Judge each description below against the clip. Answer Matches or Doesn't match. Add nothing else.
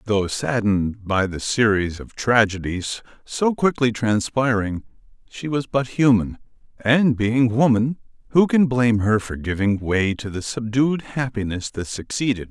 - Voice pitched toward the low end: Matches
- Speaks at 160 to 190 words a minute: Doesn't match